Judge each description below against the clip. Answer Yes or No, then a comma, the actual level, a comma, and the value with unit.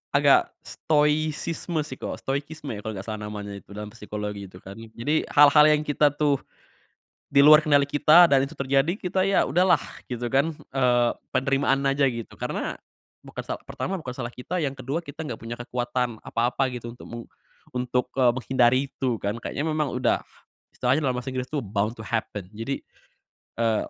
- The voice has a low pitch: Yes, low, 130 Hz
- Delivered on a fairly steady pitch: No, average, 4.0 semitones